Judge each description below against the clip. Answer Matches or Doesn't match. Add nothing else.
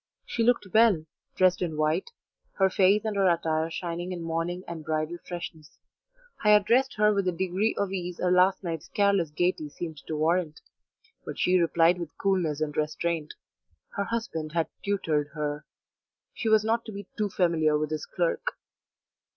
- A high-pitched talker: Doesn't match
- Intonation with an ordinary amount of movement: Matches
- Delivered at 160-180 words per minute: Matches